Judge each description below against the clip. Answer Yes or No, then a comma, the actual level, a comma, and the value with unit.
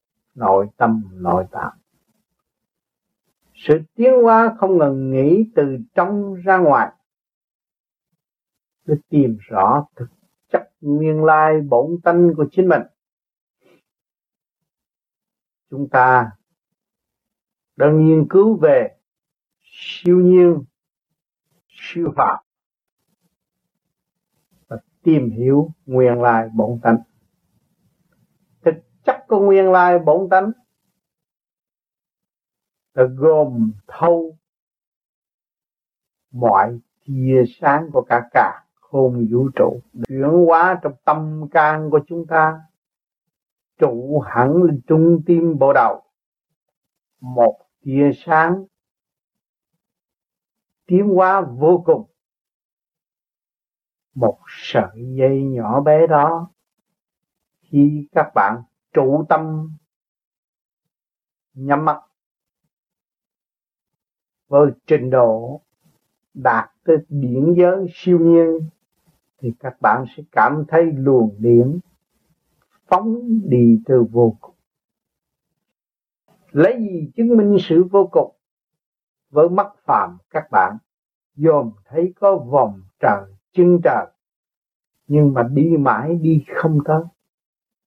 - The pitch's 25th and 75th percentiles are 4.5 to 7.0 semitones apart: Yes, average, 5.3 semitones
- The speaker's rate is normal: No, slow, 100 wpm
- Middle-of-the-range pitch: Yes, medium, 155 Hz